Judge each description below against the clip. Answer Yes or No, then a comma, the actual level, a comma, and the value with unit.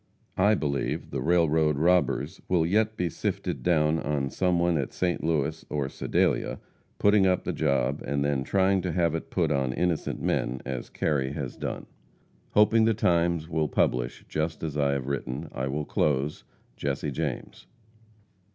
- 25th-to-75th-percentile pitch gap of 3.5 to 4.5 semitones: Yes, average, 4.1 semitones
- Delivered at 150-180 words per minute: Yes, average, 165 wpm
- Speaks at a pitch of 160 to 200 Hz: No, very low, 80 Hz